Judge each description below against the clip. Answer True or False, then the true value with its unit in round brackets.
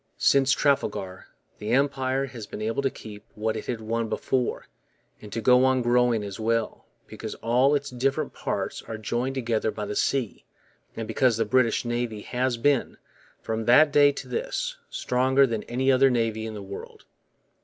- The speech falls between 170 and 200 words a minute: True (175 wpm)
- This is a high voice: False (120 Hz)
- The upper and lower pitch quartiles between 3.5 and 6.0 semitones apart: False (3.1 semitones)